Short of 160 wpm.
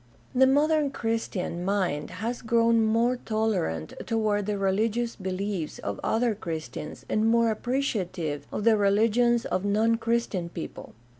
Yes: average, 140 wpm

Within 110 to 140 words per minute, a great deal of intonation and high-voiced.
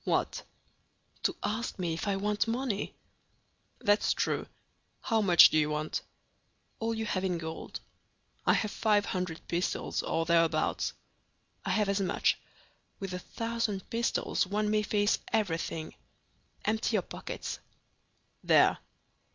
No: slow, 135 wpm; average, 4.0 semitones; high, 200 Hz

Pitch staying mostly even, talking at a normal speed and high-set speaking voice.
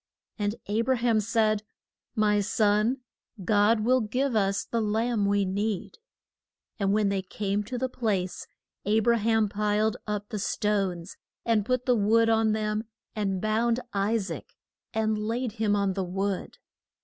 Yes: narrow, 1.9 semitones; average, 160 wpm; high, 215 Hz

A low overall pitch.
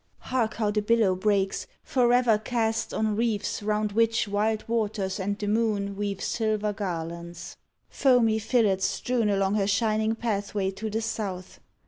No: high, 210 Hz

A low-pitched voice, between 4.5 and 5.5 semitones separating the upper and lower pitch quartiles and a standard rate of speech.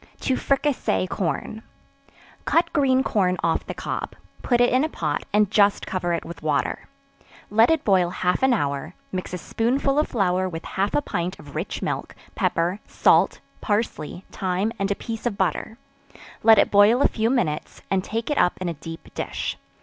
No: high, 200 Hz; average, 5.1 semitones; average, 185 wpm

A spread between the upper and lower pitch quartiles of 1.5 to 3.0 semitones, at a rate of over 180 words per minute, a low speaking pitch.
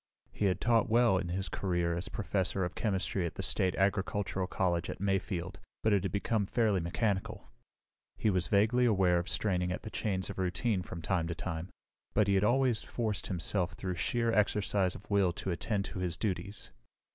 Yes: average, 2.7 semitones; average, 190 wpm; very low, 95 Hz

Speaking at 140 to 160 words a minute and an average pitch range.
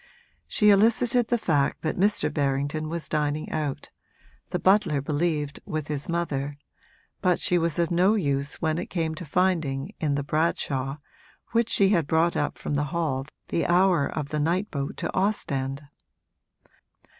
Yes: average, 155 wpm; average, 4.0 semitones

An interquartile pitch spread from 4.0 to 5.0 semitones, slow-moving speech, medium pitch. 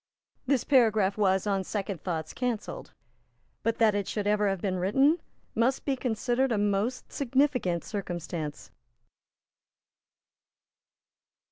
No: average, 4.5 semitones; slow, 115 wpm; high, 210 Hz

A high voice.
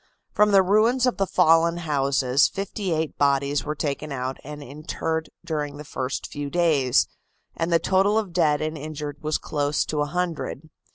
No: medium, 155 Hz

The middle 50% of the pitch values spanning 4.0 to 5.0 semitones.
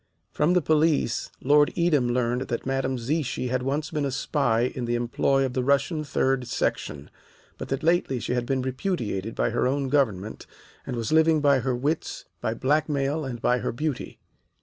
No: average, 3.3 semitones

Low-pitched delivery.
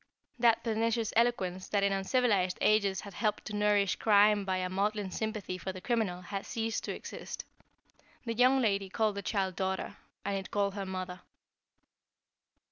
No: high, 200 Hz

